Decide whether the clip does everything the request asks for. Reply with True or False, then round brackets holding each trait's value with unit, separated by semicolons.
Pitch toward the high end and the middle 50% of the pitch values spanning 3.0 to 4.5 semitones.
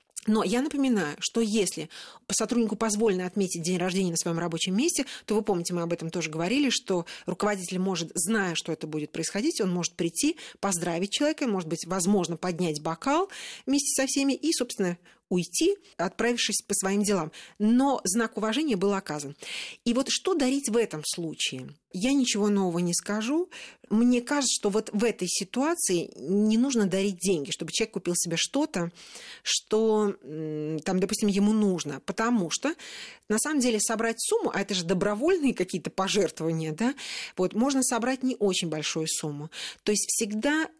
False (205 Hz; 5.3 semitones)